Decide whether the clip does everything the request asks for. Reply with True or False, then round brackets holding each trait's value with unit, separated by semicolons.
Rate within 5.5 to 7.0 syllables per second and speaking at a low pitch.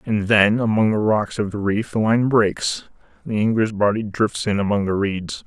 False (4.6 syllables/s; 105 Hz)